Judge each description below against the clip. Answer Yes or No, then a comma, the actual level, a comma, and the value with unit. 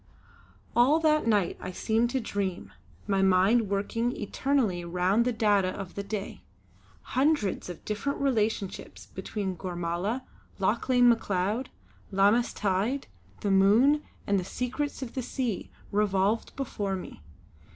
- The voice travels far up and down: No, average, 4.1 semitones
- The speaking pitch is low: No, high, 210 Hz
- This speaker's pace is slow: Yes, slow, 130 wpm